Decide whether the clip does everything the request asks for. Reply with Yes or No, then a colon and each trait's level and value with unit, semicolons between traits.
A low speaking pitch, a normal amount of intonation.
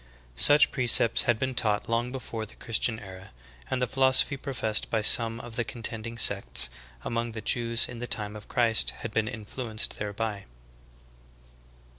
No: low, 115 Hz; narrow, 2.1 semitones